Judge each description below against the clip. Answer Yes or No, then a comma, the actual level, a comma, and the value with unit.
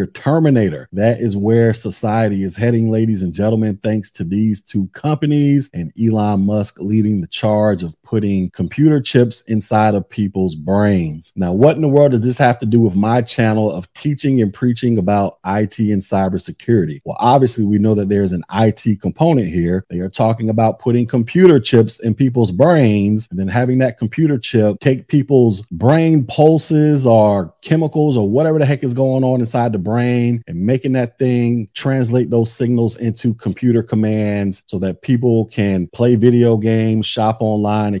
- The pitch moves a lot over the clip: No, average, 3.4 semitones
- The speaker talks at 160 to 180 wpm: Yes, average, 175 wpm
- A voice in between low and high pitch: No, low, 115 Hz